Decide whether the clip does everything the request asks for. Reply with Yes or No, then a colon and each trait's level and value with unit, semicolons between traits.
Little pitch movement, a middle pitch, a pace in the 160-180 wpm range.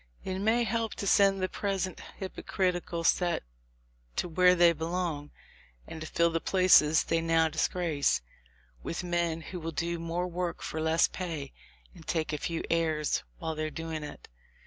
Yes: narrow, 2.2 semitones; medium, 170 Hz; average, 170 wpm